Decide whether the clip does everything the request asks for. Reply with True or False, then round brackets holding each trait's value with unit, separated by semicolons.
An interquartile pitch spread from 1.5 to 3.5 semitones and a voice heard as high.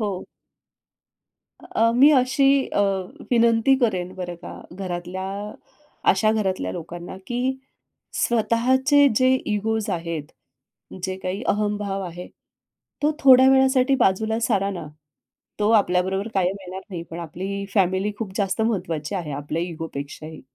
False (4.3 semitones; 195 Hz)